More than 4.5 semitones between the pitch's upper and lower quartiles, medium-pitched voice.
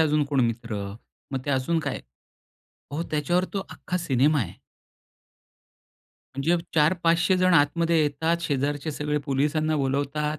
No: average, 2.8 semitones; medium, 150 Hz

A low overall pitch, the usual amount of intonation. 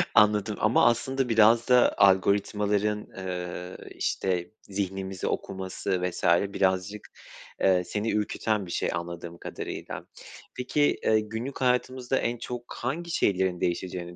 Yes: low, 100 Hz; average, 4.0 semitones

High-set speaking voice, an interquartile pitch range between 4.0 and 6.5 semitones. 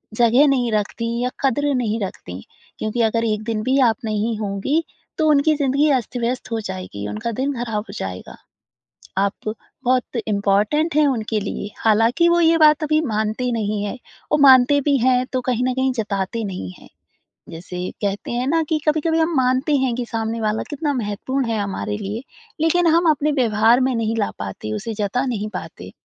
Yes: high, 235 Hz; average, 4.6 semitones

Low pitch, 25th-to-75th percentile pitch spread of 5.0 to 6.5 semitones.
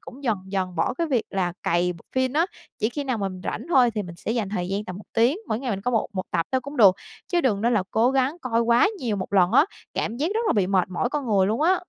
No: high, 225 Hz; average, 5.3 semitones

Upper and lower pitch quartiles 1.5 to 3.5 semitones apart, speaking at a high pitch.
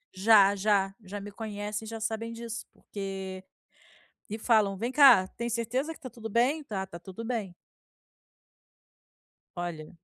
Yes: average, 3.1 semitones; high, 215 Hz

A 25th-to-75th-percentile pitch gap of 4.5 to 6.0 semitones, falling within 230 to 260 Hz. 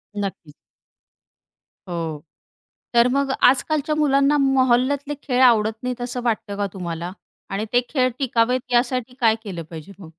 Yes: average, 4.8 semitones; high, 245 Hz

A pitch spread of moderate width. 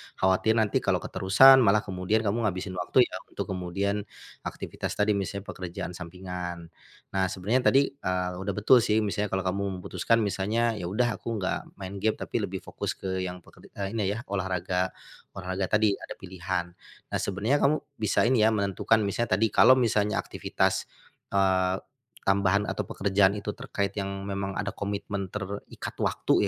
No: narrow, 2.3 semitones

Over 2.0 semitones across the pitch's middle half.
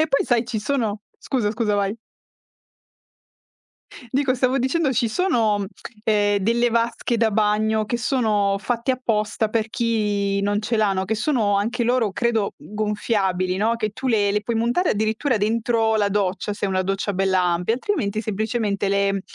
Yes: narrow, 2.6 semitones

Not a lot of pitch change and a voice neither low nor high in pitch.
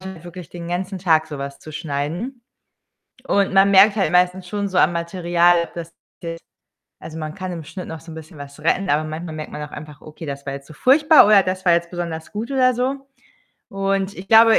No: average, 3.8 semitones; medium, 175 Hz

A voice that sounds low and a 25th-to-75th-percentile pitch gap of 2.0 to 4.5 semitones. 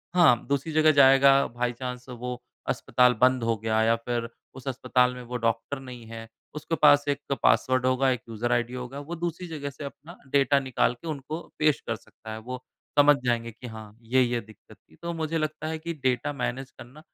Yes: low, 130 Hz; average, 3.3 semitones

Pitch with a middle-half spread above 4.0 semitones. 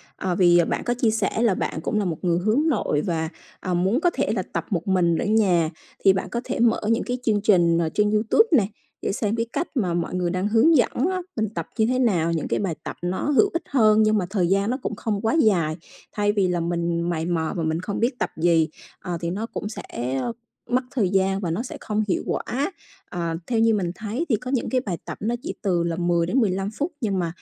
Yes: average, 4.6 semitones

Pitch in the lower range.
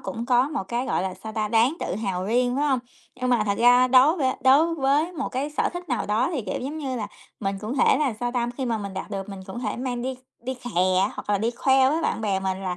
No: high, 245 Hz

